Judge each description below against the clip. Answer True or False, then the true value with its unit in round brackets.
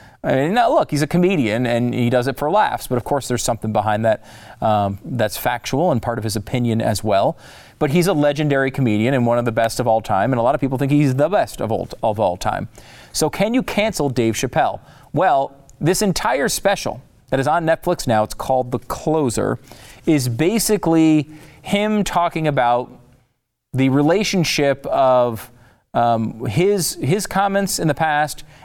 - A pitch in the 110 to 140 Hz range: True (135 Hz)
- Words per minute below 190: True (180 wpm)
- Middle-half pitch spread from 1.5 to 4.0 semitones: False (4.8 semitones)